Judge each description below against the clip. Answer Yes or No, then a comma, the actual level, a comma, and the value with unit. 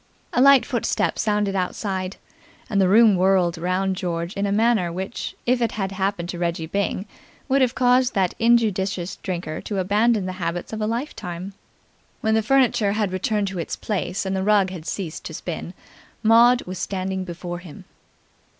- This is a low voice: No, high, 195 Hz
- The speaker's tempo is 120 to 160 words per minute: No, average, 175 wpm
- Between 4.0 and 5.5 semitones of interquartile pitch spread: No, average, 3.3 semitones